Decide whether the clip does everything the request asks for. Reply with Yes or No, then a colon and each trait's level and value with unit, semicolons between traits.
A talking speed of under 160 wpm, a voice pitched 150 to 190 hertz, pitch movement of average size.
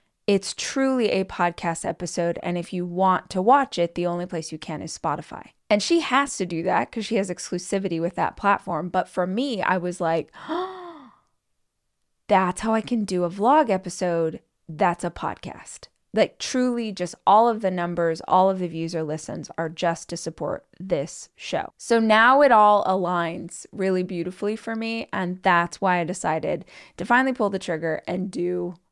No: average, 185 wpm; medium, 185 Hz; average, 3.8 semitones